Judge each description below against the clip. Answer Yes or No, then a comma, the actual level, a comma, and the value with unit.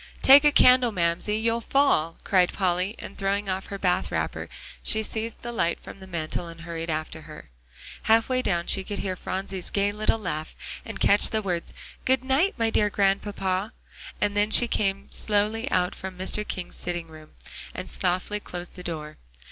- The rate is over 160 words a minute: Yes, average, 185 wpm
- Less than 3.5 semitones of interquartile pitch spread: No, average, 3.8 semitones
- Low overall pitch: No, high, 195 Hz